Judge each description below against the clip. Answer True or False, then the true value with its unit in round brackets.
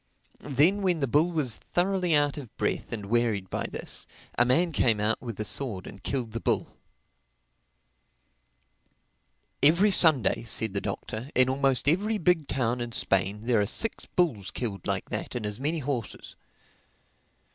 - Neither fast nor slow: True (160 wpm)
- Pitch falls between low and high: False (130 Hz)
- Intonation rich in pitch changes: True (6.2 semitones)